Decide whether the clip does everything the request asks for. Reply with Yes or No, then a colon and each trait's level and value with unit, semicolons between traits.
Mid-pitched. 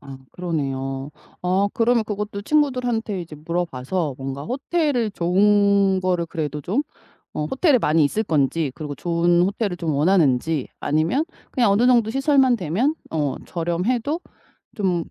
Yes: medium, 180 Hz